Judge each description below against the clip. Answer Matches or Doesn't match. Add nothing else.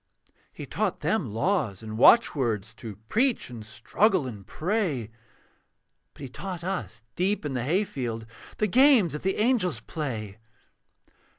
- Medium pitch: Matches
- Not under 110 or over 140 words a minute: Matches